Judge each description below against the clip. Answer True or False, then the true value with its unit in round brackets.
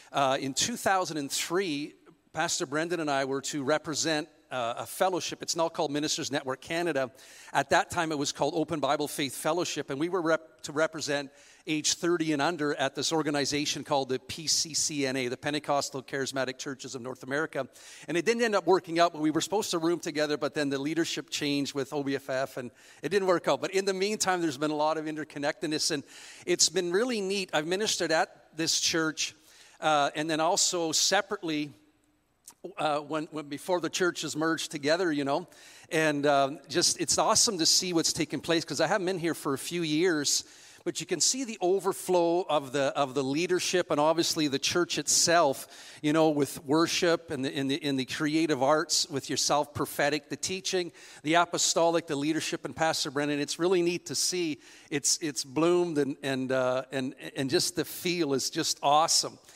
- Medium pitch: True (155 Hz)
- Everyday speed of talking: True (195 wpm)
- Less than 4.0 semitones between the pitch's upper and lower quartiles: True (3.2 semitones)